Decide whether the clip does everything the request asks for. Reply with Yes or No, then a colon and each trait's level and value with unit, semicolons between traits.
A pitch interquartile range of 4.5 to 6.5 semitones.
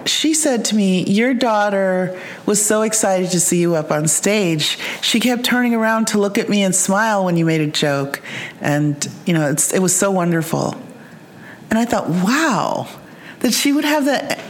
Yes: average, 4.8 semitones